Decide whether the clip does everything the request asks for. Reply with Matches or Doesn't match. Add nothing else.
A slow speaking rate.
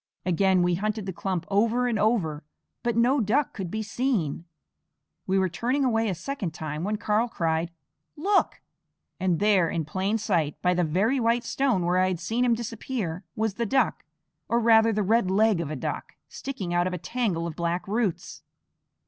Doesn't match